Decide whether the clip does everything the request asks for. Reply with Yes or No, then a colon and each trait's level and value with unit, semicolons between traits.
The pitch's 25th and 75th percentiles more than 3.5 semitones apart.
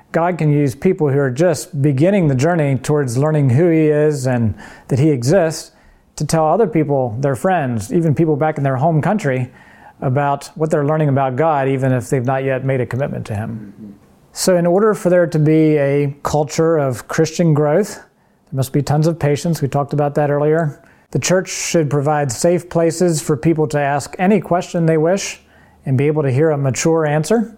No: average, 3.0 semitones